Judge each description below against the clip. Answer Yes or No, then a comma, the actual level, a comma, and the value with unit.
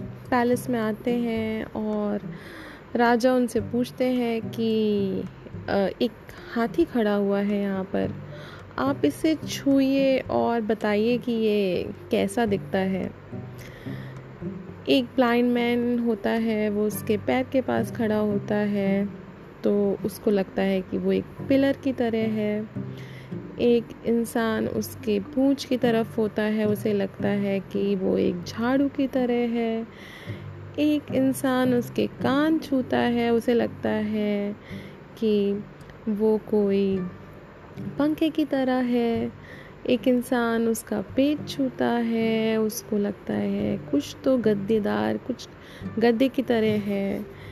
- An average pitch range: Yes, average, 3.4 semitones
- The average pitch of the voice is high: Yes, high, 225 Hz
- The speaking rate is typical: Yes, average, 130 wpm